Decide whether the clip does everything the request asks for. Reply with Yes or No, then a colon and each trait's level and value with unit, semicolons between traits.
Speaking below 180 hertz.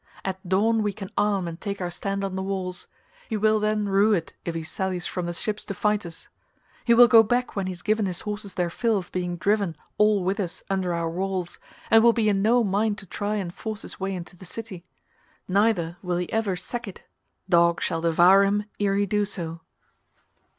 No: high, 195 Hz